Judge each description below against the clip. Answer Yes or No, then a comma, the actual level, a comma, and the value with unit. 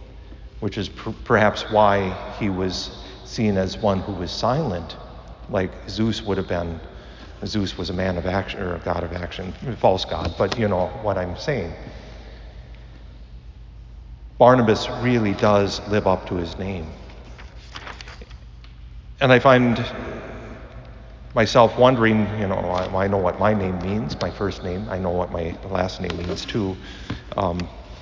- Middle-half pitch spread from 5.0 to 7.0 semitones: No, average, 3.4 semitones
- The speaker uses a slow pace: No, average, 155 wpm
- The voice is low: Yes, very low, 95 Hz